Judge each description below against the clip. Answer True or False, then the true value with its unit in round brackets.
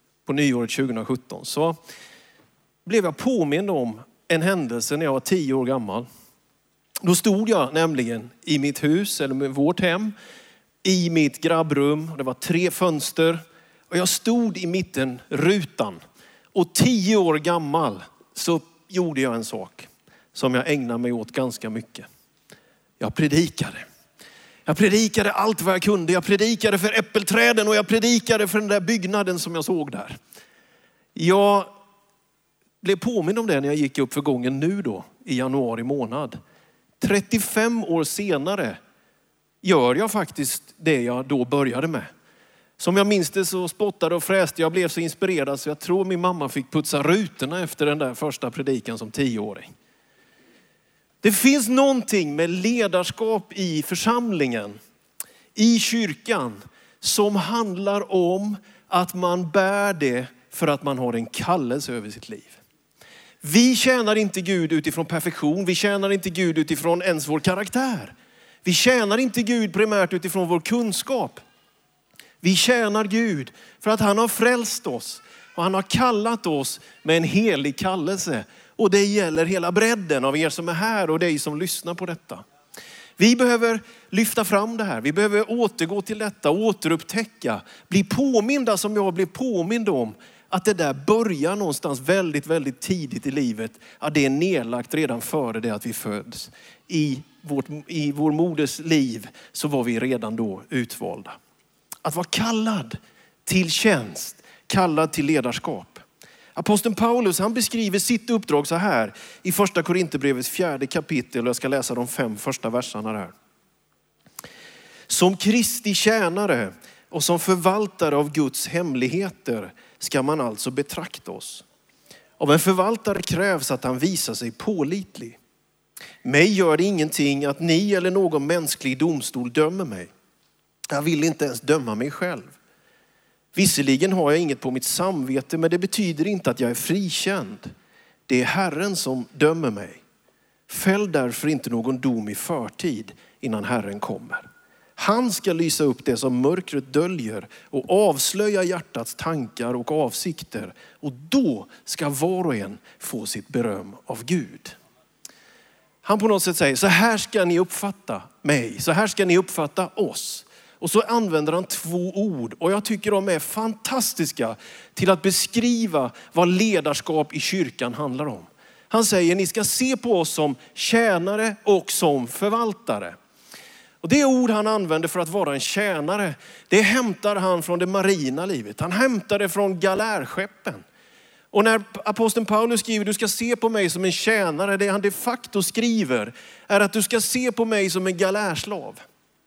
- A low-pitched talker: False (180 Hz)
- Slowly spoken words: False (155 wpm)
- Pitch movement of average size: False (5.8 semitones)